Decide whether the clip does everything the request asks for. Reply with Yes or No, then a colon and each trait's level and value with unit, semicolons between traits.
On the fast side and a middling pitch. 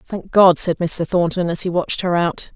Yes: fast, 235 wpm; medium, 175 Hz